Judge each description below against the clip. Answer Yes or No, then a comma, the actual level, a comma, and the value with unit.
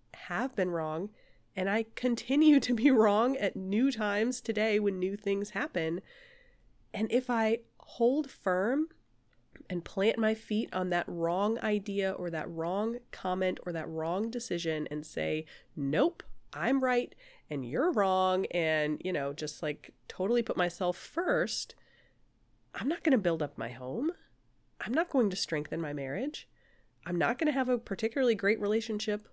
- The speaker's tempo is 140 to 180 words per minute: Yes, average, 160 wpm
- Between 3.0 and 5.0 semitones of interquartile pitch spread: No, wide, 5.6 semitones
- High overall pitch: Yes, high, 205 Hz